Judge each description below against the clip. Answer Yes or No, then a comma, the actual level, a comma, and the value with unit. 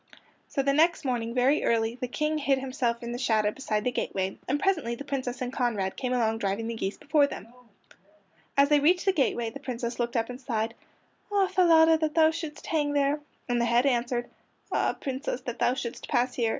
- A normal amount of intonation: Yes, average, 3.7 semitones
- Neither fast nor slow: No, fast, 210 wpm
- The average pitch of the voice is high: Yes, very high, 255 Hz